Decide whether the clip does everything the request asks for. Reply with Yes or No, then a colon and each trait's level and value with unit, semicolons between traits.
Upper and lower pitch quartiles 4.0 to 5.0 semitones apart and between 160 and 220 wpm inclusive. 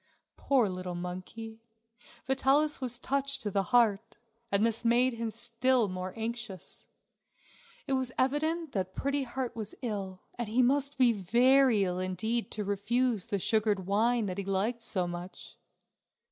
No: average, 4.5 semitones; average, 150 wpm